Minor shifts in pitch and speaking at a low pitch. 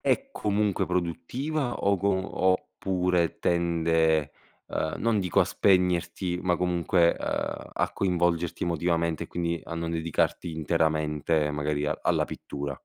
Yes: narrow, 2.3 semitones; very low, 85 Hz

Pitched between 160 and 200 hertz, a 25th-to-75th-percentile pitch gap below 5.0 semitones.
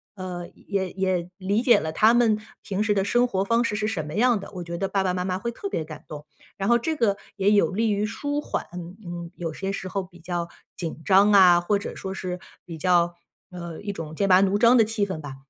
Yes: high, 190 Hz; average, 3.2 semitones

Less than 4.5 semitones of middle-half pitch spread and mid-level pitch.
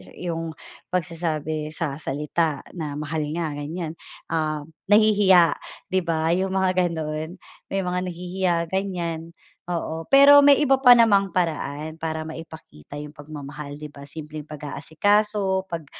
Yes: average, 3.6 semitones; medium, 165 Hz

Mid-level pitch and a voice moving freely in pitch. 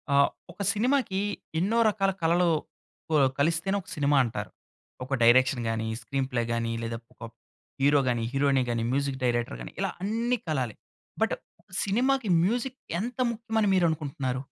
Yes: medium, 145 Hz; wide, 8.1 semitones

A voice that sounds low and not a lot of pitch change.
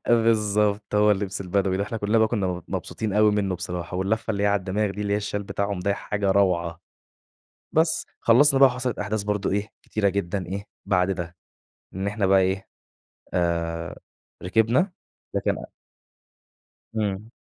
Yes: low, 100 Hz; narrow, 2.2 semitones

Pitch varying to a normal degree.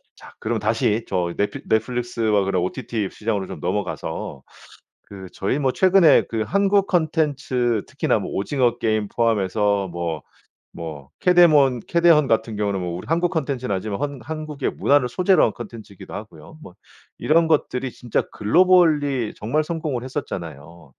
No: wide, 6.9 semitones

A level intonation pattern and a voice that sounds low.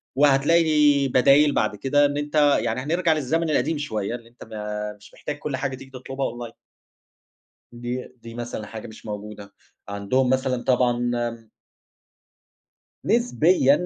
No: average, 4.0 semitones; low, 130 Hz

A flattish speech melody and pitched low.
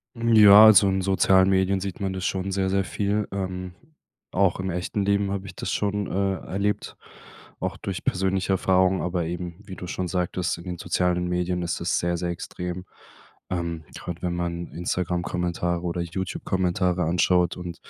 Yes: narrow, 1.6 semitones; very low, 90 Hz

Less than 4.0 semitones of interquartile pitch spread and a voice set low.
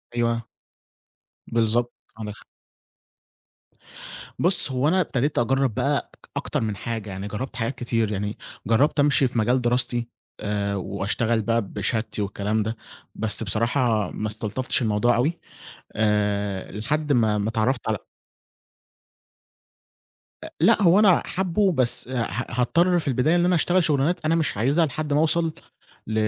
No: average, 5.2 semitones; low, 120 Hz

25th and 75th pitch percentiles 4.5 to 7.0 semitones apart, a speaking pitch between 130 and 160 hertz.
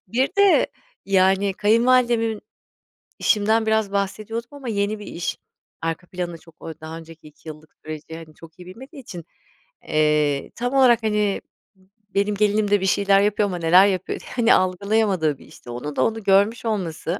No: average, 4.9 semitones; high, 200 Hz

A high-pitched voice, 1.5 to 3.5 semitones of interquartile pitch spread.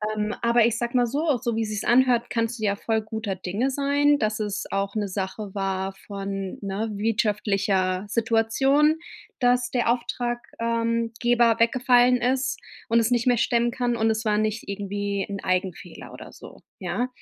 Yes: high, 225 Hz; average, 3.1 semitones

